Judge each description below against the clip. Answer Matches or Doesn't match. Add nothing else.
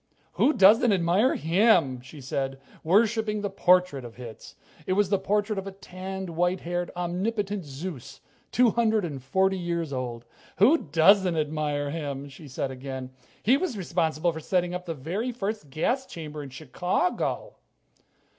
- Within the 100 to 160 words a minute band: Matches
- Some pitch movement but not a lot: Doesn't match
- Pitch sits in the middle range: Matches